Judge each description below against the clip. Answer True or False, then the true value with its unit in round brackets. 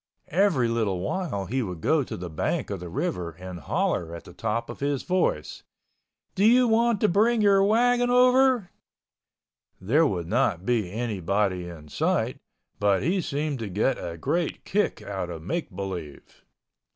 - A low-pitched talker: True (115 Hz)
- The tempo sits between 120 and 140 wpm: False (165 wpm)